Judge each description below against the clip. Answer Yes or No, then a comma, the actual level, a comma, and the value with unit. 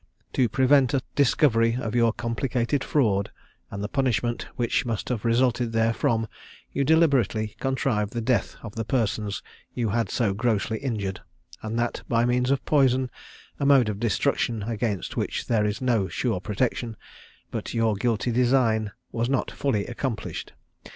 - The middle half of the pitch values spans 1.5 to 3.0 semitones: Yes, average, 2.7 semitones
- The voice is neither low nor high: No, low, 115 Hz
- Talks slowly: No, average, 155 wpm